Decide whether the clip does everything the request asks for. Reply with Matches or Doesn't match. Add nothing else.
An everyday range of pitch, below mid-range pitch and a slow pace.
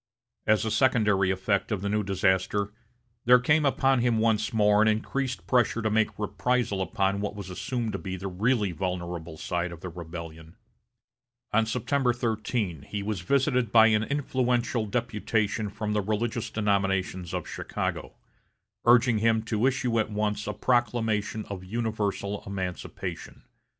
Doesn't match